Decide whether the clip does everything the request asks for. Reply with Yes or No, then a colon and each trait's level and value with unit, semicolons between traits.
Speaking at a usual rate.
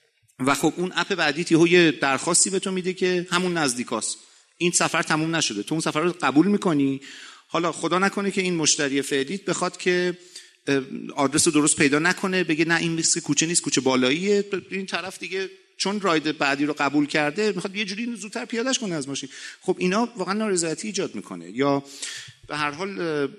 No: fast, 185 wpm